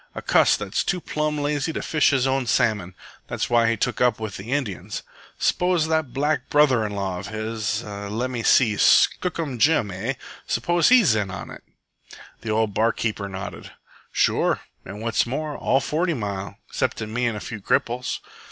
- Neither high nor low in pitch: No, low, 115 Hz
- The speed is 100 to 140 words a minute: No, average, 180 wpm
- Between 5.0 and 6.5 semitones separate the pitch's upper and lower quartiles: Yes, wide, 5.6 semitones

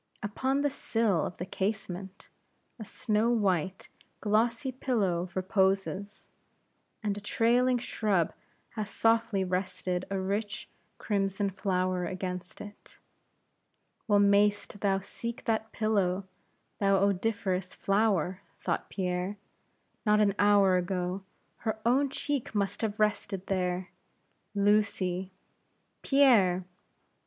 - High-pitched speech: Yes, high, 200 Hz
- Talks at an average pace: No, slow, 110 wpm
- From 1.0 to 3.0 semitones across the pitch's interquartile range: Yes, average, 2.7 semitones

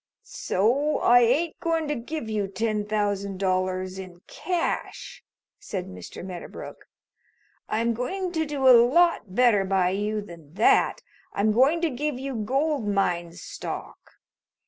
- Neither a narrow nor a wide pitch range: No, wide, 6.5 semitones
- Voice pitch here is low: No, high, 220 Hz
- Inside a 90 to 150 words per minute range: Yes, average, 140 wpm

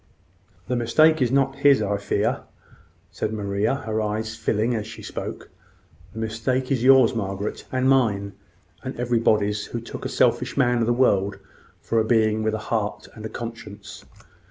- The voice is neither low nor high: No, low, 115 Hz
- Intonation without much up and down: No, average, 3.0 semitones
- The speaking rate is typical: Yes, average, 170 wpm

